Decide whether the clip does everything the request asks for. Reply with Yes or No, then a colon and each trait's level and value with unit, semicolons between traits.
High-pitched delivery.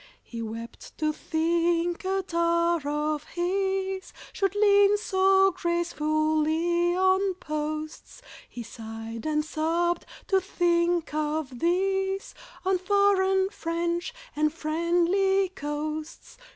Yes: very high, 340 Hz